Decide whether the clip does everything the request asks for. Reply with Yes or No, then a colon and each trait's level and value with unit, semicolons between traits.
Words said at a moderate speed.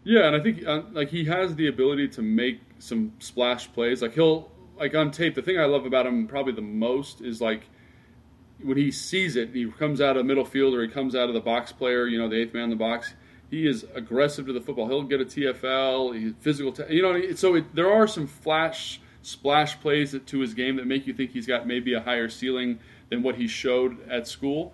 No: fast, 240 wpm